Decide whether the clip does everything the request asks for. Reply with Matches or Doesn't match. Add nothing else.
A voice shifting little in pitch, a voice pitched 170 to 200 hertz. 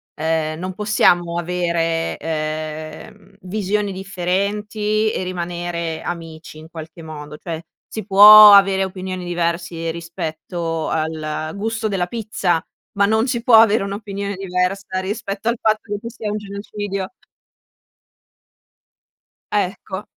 Doesn't match